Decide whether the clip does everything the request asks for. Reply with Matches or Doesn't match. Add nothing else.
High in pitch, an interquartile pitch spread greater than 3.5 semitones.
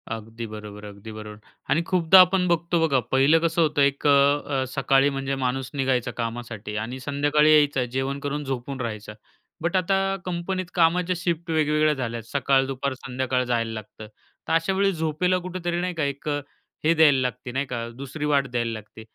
Doesn't match